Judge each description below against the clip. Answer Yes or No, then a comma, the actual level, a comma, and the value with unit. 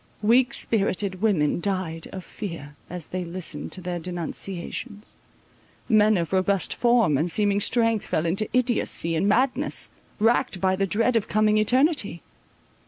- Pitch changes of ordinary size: Yes, average, 4.2 semitones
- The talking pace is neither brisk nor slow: Yes, average, 145 wpm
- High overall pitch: Yes, high, 200 Hz